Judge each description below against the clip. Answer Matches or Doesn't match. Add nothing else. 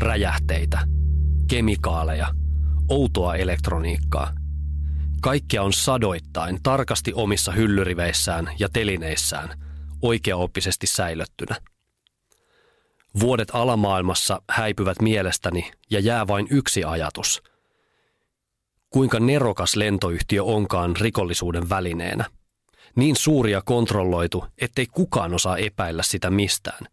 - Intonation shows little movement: Doesn't match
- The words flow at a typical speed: Doesn't match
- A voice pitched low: Matches